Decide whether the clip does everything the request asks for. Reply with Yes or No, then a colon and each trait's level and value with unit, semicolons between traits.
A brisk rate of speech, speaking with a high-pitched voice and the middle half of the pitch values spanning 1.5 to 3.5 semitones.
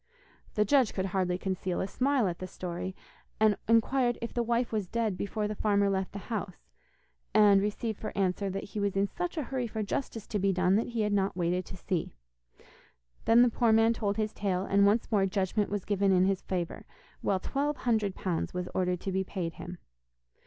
Yes: fast, 210 wpm; high, 200 Hz; average, 3.1 semitones